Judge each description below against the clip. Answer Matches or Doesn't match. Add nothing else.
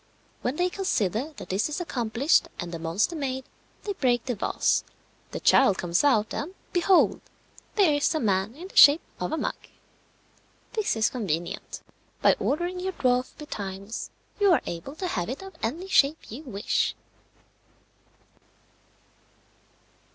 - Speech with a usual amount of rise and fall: Doesn't match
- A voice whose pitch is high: Matches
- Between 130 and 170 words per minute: Matches